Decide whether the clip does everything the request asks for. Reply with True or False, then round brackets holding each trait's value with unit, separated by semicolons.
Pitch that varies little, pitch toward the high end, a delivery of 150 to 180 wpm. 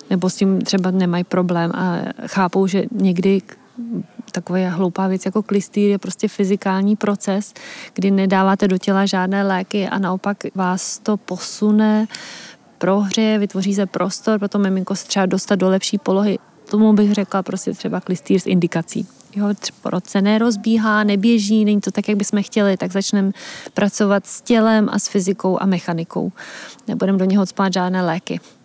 True (1.8 semitones; 195 Hz; 155 wpm)